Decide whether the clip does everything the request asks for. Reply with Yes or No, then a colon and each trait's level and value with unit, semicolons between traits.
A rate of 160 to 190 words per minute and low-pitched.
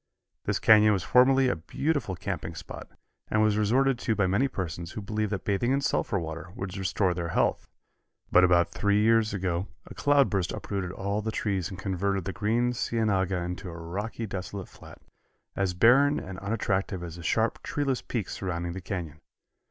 Yes: average, 180 wpm; low, 100 Hz